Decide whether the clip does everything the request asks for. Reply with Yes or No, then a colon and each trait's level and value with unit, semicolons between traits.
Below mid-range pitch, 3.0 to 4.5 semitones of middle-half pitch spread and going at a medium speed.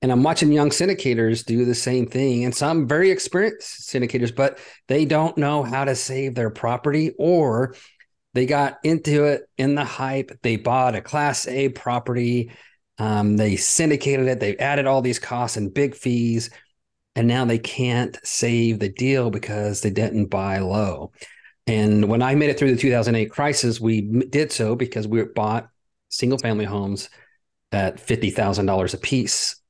Yes: low, 125 Hz; average, 3.5 semitones; average, 170 wpm